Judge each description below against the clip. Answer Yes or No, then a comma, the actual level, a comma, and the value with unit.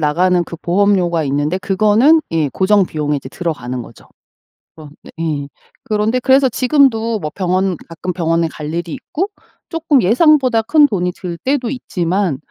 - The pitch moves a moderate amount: No, wide, 6.0 semitones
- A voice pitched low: No, medium, 185 Hz